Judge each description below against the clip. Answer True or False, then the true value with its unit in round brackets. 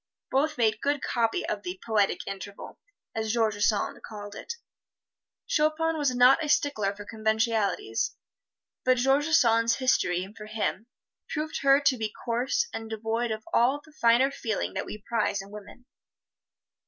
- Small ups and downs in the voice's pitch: False (4.4 semitones)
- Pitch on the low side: False (230 Hz)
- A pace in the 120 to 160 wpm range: True (155 wpm)